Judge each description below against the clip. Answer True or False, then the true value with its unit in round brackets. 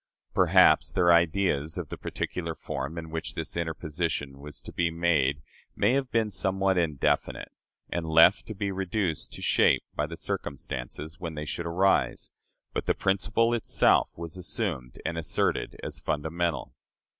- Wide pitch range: False (3.5 semitones)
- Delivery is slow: False (155 wpm)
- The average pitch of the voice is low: True (85 Hz)